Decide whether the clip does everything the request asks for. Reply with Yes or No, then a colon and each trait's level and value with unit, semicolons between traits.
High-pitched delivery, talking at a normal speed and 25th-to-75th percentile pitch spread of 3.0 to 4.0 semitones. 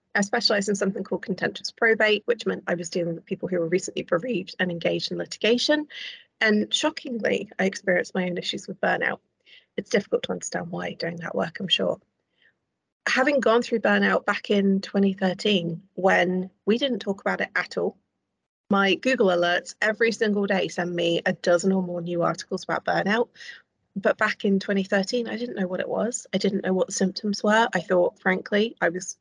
Yes: high, 195 Hz; average, 195 wpm; average, 3.3 semitones